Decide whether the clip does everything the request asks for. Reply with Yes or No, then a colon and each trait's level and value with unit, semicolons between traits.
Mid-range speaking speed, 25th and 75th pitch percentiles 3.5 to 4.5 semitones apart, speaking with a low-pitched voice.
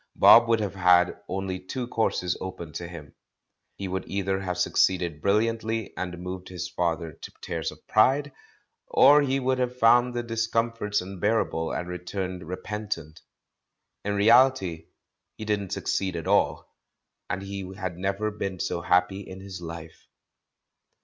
Yes: average, 150 wpm; average, 3.8 semitones; very low, 95 Hz